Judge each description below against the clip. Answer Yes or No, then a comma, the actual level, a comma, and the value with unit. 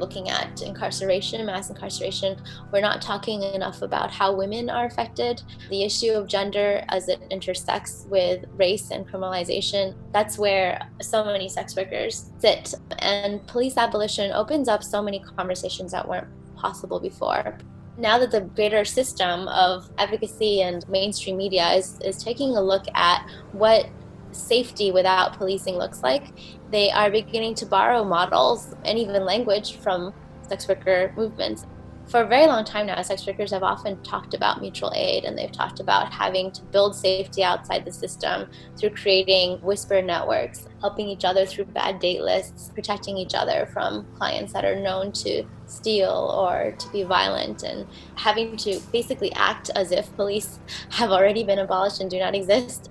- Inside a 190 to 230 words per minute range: No, average, 165 wpm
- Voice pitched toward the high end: Yes, high, 200 Hz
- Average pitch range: No, narrow, 2.1 semitones